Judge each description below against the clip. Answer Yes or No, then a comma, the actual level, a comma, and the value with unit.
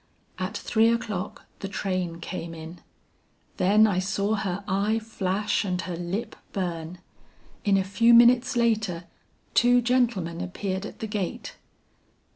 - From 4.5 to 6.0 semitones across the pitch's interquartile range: No, average, 3.4 semitones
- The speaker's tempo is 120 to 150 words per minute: Yes, slow, 135 wpm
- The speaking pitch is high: Yes, high, 200 Hz